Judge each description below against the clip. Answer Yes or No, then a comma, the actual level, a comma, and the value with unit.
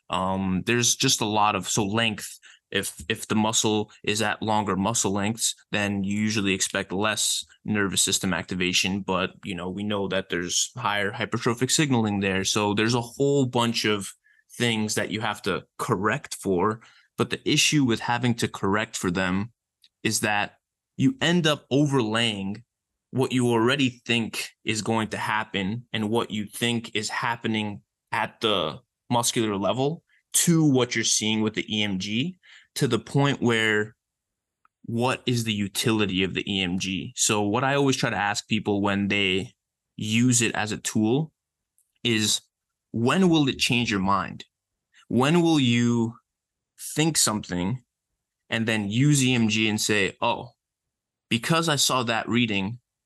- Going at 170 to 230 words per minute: No, average, 155 wpm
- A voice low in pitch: Yes, low, 110 Hz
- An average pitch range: Yes, average, 3.1 semitones